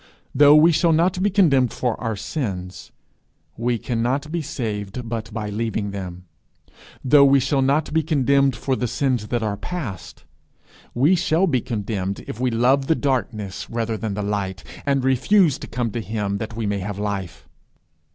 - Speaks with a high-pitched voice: No, low, 120 Hz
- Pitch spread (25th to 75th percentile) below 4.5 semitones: No, average, 5.1 semitones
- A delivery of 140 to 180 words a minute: Yes, average, 175 wpm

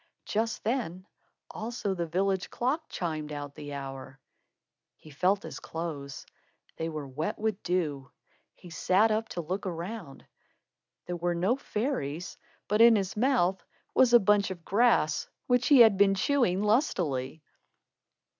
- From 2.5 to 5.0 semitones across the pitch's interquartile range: No, wide, 5.6 semitones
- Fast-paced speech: No, average, 145 wpm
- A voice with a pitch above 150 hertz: Yes, medium, 185 Hz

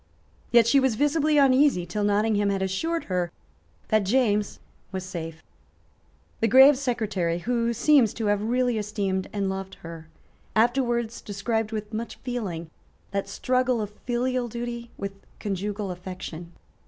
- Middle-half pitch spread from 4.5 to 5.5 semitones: No, average, 4.0 semitones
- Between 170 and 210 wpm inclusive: No, average, 140 wpm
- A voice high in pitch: Yes, high, 215 Hz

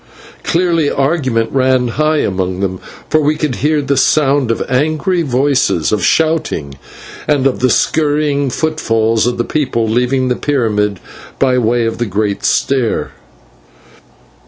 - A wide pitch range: No, average, 4.8 semitones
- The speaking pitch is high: No, low, 130 Hz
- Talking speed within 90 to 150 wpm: Yes, average, 140 wpm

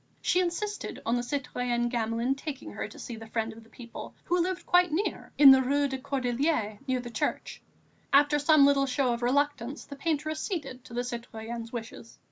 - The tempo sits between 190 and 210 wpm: Yes, average, 195 wpm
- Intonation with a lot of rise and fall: No, average, 3.6 semitones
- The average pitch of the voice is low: No, very high, 260 Hz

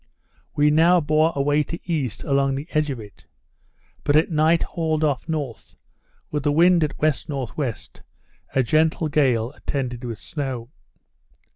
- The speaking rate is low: No, average, 145 wpm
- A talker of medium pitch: Yes, medium, 150 Hz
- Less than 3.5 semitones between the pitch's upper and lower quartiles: Yes, average, 2.8 semitones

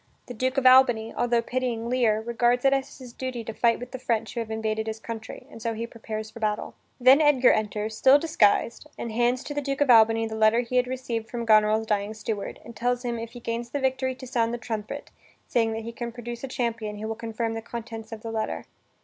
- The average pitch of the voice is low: No, high, 230 Hz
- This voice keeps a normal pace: No, fast, 240 wpm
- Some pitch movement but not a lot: No, narrow, 2.1 semitones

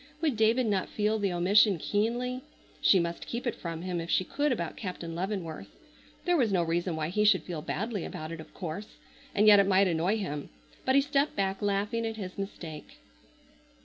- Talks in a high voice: Yes, high, 195 Hz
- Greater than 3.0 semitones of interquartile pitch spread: Yes, average, 4.4 semitones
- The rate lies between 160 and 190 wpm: No, average, 200 wpm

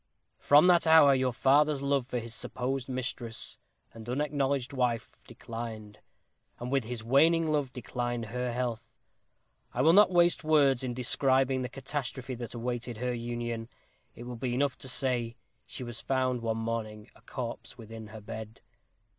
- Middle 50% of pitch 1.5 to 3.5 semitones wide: Yes, average, 2.7 semitones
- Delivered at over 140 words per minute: Yes, average, 160 wpm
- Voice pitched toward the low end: Yes, low, 125 Hz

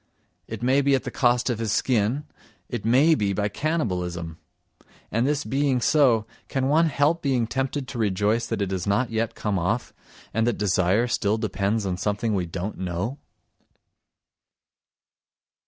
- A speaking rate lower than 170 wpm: Yes, average, 160 wpm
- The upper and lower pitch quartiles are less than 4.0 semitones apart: No, average, 4.7 semitones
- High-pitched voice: No, low, 115 Hz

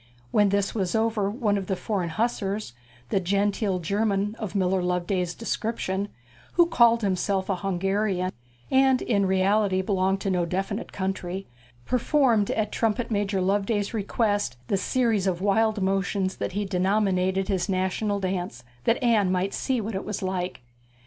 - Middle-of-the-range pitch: No, high, 195 Hz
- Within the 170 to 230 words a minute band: No, average, 155 wpm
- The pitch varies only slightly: Yes, narrow, 2.3 semitones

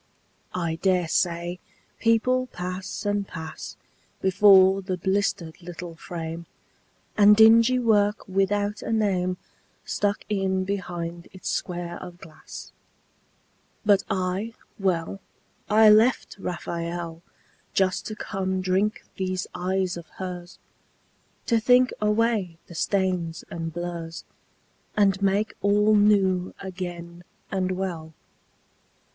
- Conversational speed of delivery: No, slow, 110 wpm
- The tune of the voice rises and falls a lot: No, average, 2.8 semitones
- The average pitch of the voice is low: No, high, 190 Hz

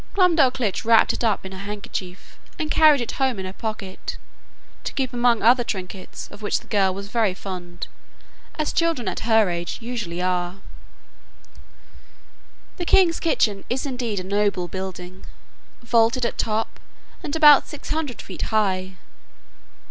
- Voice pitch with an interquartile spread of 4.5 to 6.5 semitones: Yes, average, 5.1 semitones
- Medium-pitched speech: No, high, 220 Hz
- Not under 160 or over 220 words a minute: No, average, 150 wpm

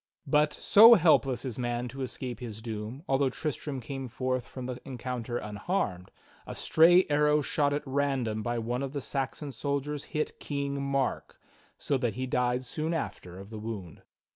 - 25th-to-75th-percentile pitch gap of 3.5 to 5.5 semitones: No, average, 3.1 semitones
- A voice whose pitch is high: No, low, 130 Hz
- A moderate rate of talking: Yes, average, 170 wpm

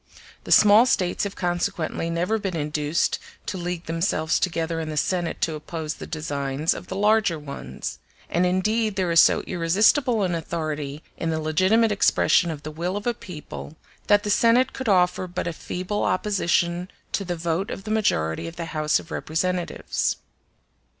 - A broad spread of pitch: No, average, 3.8 semitones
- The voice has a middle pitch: Yes, medium, 175 Hz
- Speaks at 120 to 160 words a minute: No, average, 175 wpm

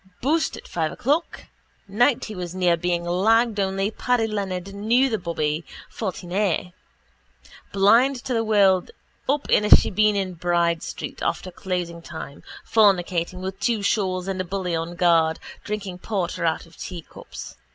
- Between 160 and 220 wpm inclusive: No, average, 150 wpm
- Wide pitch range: No, average, 3.5 semitones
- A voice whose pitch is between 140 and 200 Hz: Yes, high, 190 Hz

